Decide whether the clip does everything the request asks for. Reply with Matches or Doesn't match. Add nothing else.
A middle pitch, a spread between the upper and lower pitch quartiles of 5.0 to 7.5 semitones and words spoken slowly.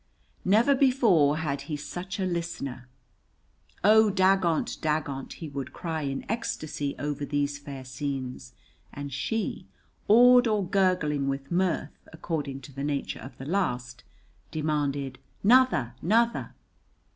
Matches